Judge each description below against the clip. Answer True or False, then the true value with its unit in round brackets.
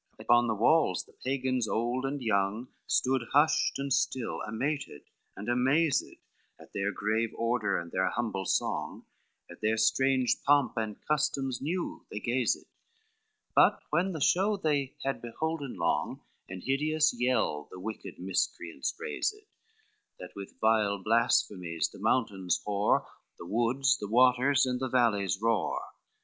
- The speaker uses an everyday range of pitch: True (4.6 semitones)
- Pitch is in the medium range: False (120 Hz)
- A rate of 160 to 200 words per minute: False (145 wpm)